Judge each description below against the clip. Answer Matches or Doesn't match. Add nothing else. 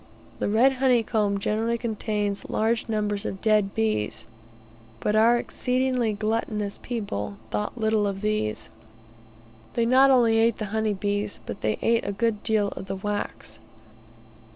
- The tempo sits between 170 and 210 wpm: Doesn't match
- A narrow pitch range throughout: Matches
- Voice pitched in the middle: Doesn't match